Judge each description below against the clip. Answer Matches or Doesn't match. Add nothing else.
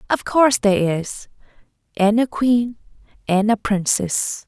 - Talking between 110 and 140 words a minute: Matches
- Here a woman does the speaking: Matches